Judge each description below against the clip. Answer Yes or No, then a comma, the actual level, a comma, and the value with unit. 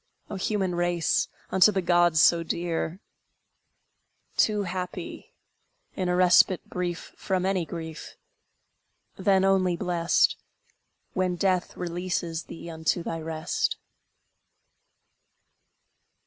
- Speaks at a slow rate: Yes, slow, 100 wpm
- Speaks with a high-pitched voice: No, medium, 180 Hz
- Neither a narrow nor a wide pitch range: No, narrow, 1.7 semitones